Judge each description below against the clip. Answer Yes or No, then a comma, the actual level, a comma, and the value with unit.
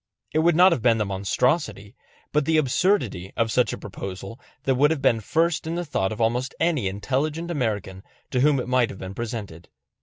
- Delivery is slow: No, fast, 205 wpm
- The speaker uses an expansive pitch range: Yes, wide, 7.0 semitones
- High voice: No, low, 125 Hz